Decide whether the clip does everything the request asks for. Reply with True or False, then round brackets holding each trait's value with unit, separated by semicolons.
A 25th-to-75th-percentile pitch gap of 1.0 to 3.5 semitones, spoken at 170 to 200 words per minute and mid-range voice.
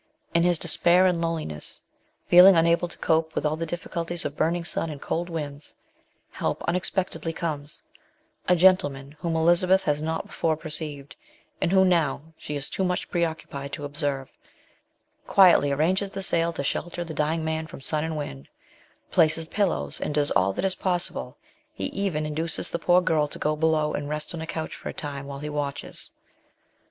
True (2.8 semitones; 185 wpm; 160 Hz)